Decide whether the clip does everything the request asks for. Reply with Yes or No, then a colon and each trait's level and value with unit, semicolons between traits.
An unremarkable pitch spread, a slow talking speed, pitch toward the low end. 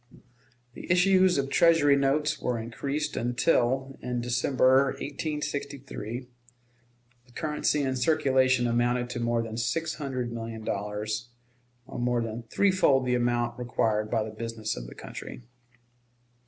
Yes: average, 3.1 semitones; slow, 130 wpm; low, 125 Hz